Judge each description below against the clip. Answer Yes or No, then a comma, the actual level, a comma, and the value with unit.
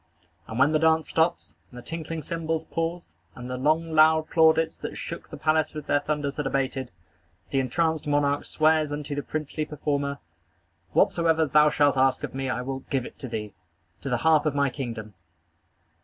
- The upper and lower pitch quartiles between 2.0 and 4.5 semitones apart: Yes, average, 2.9 semitones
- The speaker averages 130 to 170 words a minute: No, average, 185 wpm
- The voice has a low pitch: No, medium, 150 Hz